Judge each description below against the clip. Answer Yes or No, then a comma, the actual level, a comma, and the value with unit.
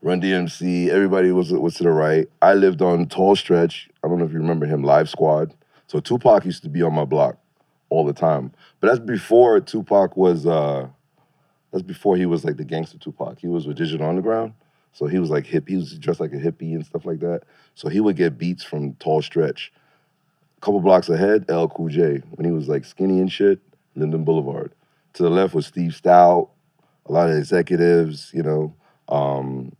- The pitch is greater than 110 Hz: No, very low, 85 Hz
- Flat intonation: No, average, 3.2 semitones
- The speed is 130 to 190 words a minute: No, fast, 205 wpm